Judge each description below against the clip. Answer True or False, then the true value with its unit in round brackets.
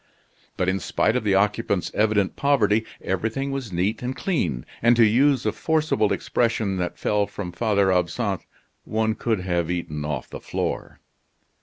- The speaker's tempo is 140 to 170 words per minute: True (160 wpm)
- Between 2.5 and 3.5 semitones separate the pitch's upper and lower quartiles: False (4.4 semitones)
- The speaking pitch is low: True (105 Hz)